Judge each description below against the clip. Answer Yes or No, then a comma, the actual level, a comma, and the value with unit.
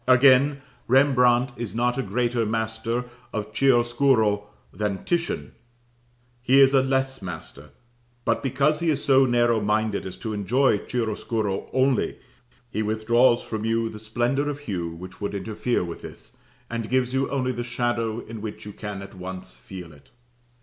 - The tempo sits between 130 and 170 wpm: Yes, average, 160 wpm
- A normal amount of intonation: Yes, average, 3.7 semitones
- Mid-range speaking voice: No, low, 120 Hz